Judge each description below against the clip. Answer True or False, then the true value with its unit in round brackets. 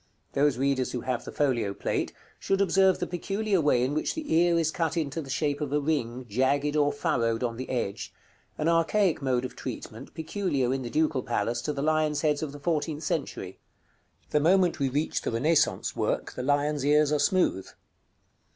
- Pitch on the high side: False (145 Hz)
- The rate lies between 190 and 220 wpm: True (195 wpm)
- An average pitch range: True (3.7 semitones)